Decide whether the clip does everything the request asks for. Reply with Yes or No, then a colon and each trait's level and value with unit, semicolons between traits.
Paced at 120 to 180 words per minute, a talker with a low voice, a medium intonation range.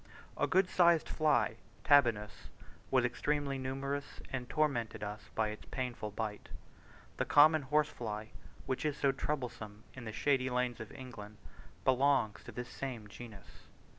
Yes: average, 140 wpm; low, 125 Hz; average, 4.4 semitones